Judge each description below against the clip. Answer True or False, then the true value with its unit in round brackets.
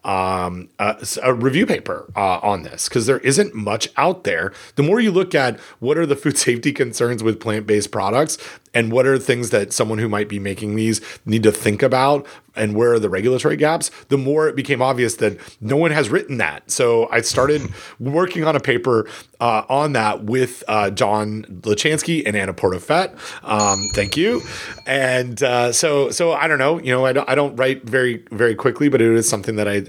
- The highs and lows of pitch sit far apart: False (5.0 semitones)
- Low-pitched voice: True (120 Hz)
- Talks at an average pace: False (210 wpm)